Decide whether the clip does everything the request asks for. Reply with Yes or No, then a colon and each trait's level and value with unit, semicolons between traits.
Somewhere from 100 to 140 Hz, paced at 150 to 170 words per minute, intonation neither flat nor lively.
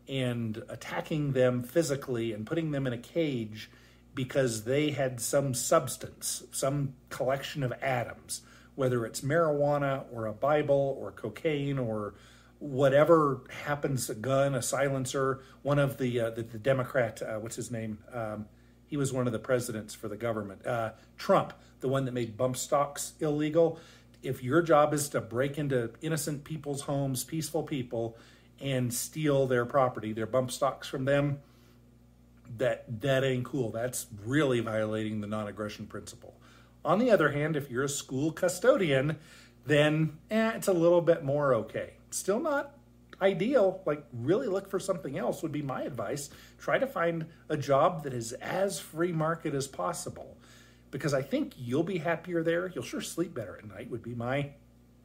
Yes: low, 135 Hz; average, 165 wpm; average, 4.3 semitones